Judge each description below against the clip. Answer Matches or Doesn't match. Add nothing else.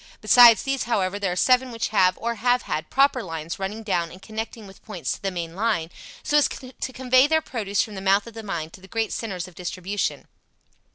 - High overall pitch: Matches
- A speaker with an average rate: Doesn't match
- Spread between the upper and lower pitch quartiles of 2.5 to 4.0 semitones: Doesn't match